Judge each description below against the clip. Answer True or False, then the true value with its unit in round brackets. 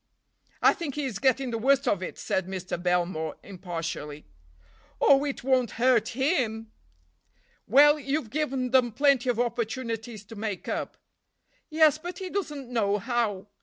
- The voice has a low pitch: False (240 Hz)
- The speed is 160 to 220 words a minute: False (150 wpm)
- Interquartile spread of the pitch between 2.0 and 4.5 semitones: False (5.1 semitones)